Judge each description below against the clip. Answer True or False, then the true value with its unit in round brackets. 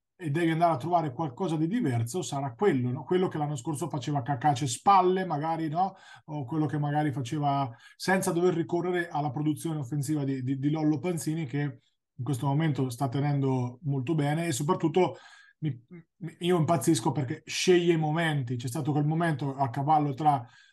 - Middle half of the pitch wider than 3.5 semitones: False (3.0 semitones)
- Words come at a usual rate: False (175 wpm)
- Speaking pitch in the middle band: True (155 Hz)